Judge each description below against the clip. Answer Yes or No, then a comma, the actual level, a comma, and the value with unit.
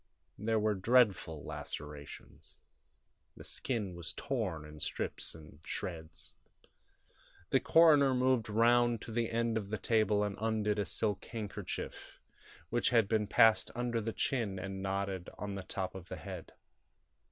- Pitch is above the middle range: No, low, 105 Hz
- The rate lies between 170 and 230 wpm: No, average, 145 wpm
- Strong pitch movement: No, average, 3.4 semitones